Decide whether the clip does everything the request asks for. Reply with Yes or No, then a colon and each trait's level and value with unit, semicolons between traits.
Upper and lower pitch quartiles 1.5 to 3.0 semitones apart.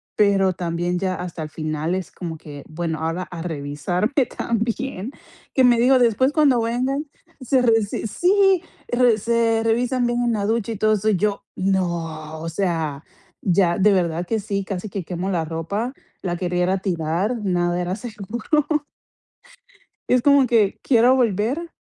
No: wide, 5.4 semitones